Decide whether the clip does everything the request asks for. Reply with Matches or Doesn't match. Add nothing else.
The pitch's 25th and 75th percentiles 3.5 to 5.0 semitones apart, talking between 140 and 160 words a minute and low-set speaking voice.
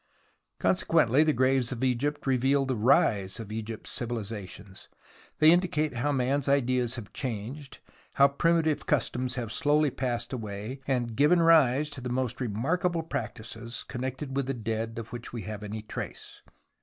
Matches